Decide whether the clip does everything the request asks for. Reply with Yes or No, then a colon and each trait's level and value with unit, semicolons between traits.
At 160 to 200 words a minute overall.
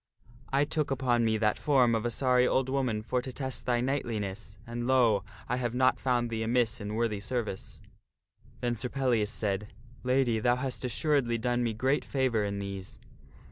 Yes: average, 185 wpm